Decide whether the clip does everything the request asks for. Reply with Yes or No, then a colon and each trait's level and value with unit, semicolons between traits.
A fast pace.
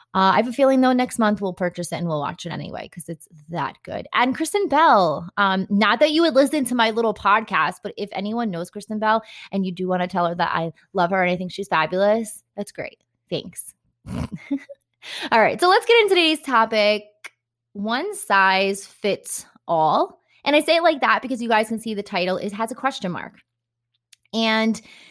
Yes: fast, 215 wpm